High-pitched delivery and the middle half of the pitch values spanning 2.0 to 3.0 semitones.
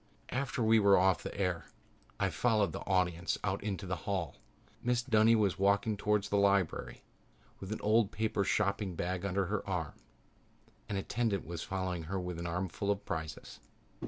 No: low, 100 Hz; average, 2.7 semitones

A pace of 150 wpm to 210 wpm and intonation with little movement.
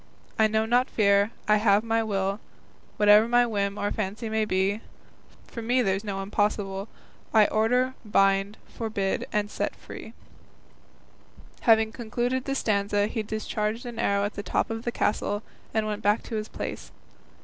Yes: average, 155 wpm; narrow, 1.9 semitones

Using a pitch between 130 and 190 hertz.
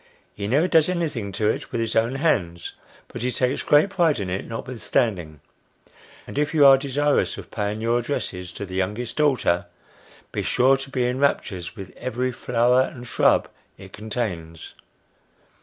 No: low, 120 Hz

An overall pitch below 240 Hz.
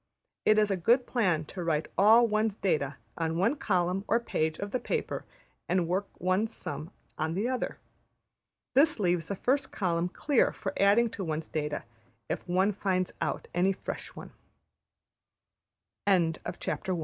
Yes: high, 190 Hz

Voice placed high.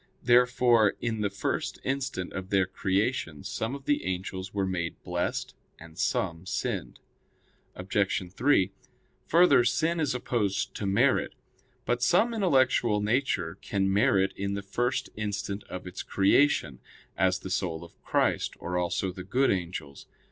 No: low, 100 Hz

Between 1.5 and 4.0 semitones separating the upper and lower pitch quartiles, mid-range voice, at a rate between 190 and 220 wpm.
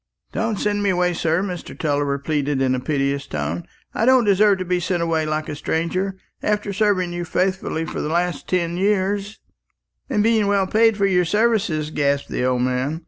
No: average, 5.1 semitones; medium, 180 Hz; average, 195 wpm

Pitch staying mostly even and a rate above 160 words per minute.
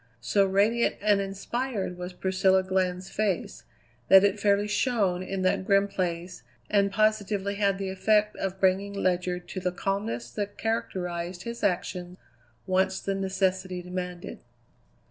No: narrow, 1.8 semitones; average, 140 wpm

